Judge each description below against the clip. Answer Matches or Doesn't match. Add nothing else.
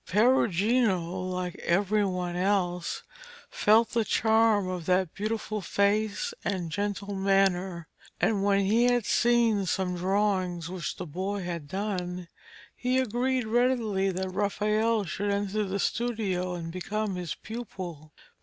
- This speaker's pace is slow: Matches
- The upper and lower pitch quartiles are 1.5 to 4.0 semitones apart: Matches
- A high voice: Matches